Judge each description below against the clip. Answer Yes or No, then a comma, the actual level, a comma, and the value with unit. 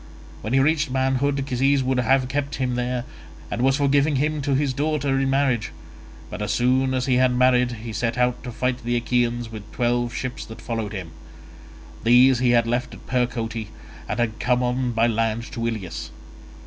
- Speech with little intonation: Yes, narrow, 2.0 semitones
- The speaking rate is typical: Yes, average, 190 wpm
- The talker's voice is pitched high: No, low, 125 Hz